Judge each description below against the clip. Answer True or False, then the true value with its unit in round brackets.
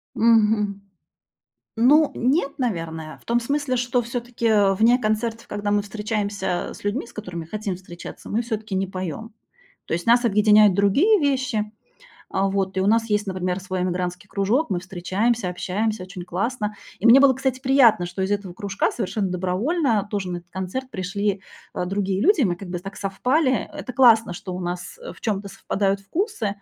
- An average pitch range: True (3.9 semitones)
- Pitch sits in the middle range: False (205 Hz)